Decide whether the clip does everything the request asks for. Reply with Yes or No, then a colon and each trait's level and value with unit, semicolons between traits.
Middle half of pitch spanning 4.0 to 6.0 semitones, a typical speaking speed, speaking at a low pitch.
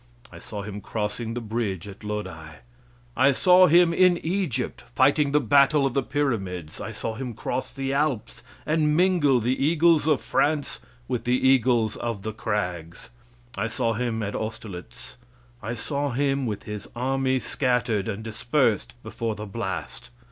Yes: average, 4.9 semitones; average, 160 wpm; low, 120 Hz